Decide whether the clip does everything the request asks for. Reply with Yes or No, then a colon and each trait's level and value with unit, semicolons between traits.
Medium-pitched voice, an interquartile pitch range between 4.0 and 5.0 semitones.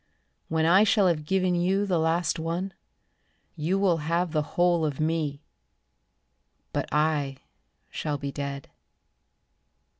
No: medium, 165 Hz; average, 3.0 semitones